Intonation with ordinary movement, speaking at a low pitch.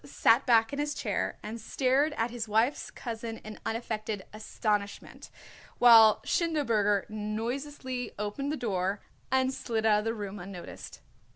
No: average, 3.4 semitones; high, 225 Hz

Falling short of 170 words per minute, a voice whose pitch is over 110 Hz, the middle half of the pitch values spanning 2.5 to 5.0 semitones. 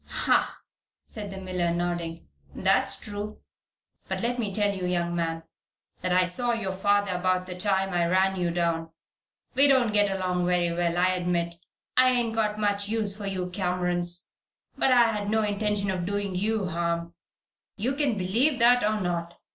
No: average, 175 wpm; high, 190 Hz; average, 3.1 semitones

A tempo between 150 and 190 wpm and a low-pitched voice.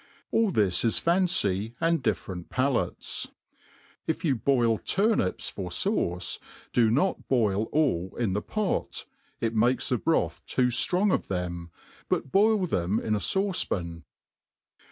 No: average, 140 wpm; low, 120 Hz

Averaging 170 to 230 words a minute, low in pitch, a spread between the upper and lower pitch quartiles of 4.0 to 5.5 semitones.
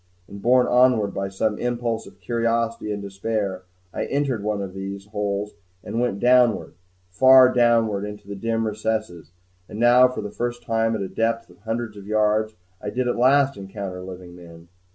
No: average, 180 wpm; low, 110 Hz; average, 3.2 semitones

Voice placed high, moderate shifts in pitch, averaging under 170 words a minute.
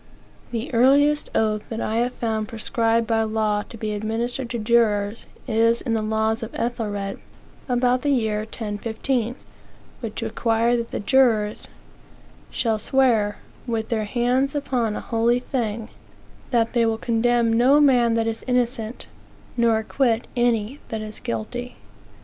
No: high, 230 Hz; narrow, 1.8 semitones; average, 145 wpm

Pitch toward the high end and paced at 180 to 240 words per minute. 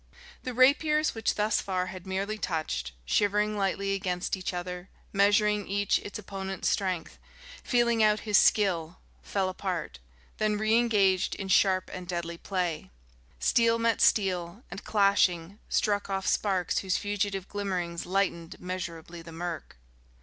No: high, 195 Hz; average, 140 wpm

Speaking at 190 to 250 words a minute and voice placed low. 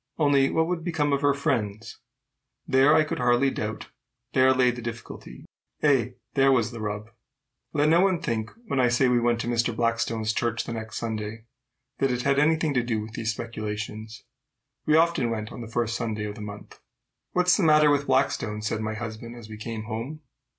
Yes: average, 200 wpm; low, 120 Hz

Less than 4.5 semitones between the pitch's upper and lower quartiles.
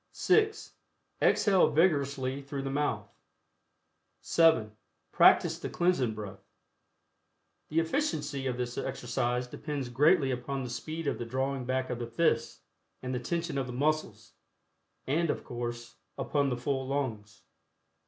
Yes: average, 3.8 semitones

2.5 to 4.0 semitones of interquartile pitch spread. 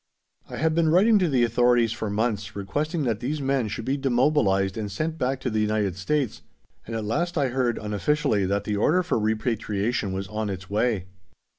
No: average, 5.1 semitones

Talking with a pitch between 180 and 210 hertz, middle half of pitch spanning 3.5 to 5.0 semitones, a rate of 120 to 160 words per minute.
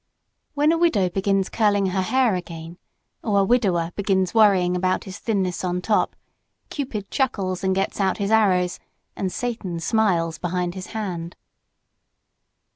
No: high, 190 Hz; average, 3.1 semitones; average, 145 wpm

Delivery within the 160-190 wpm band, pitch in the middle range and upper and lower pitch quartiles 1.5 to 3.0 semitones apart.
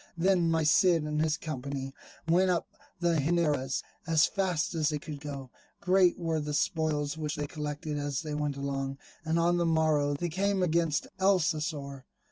Yes: average, 170 wpm; medium, 155 Hz; narrow, 2.6 semitones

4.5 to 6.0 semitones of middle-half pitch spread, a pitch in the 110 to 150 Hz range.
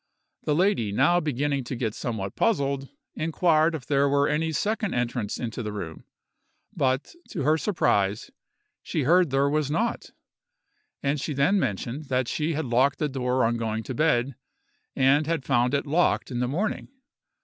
No: average, 4.1 semitones; medium, 140 Hz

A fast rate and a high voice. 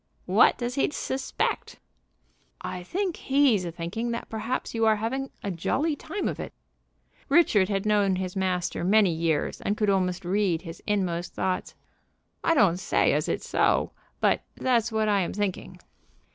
No: average, 165 wpm; high, 205 Hz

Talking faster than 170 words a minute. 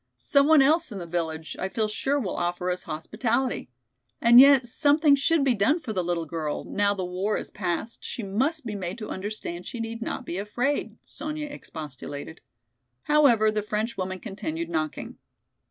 Yes: average, 180 wpm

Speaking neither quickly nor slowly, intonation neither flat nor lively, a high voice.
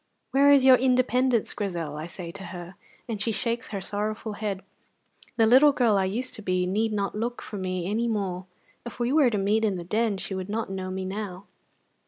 No: fast, 215 wpm; average, 3.8 semitones; high, 210 Hz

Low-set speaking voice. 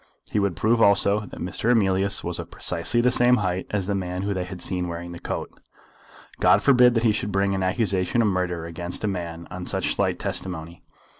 Yes: very low, 95 Hz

